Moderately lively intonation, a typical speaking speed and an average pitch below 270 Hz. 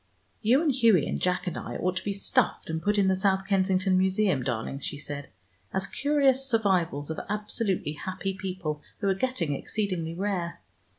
Yes: average, 3.6 semitones; average, 180 wpm; high, 190 Hz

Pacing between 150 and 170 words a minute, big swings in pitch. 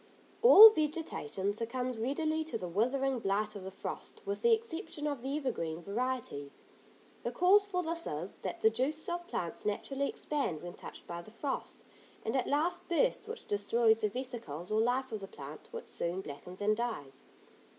No: average, 180 wpm; wide, 7.5 semitones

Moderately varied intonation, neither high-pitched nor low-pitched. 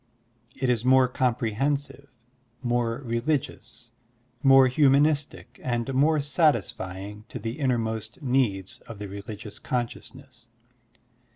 No: average, 3.3 semitones; low, 125 Hz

